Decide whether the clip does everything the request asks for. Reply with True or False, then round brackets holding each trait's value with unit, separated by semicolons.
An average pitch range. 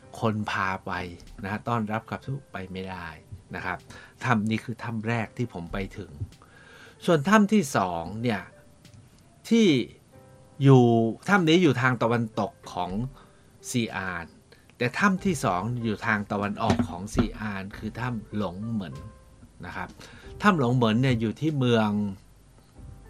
True (3.7 semitones)